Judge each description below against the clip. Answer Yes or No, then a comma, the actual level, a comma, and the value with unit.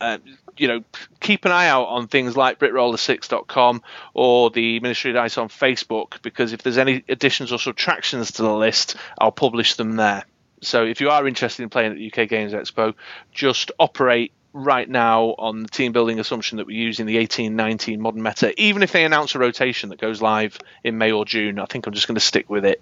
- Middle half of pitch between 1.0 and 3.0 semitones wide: Yes, average, 2.7 semitones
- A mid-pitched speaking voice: No, low, 120 Hz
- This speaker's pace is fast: Yes, fast, 220 wpm